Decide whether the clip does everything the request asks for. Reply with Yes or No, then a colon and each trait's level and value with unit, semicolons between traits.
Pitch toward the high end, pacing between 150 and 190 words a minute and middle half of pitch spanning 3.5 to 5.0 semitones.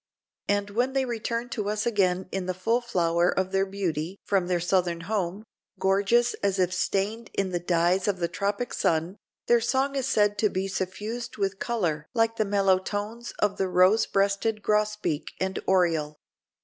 No: high, 195 Hz; average, 175 wpm; average, 3.1 semitones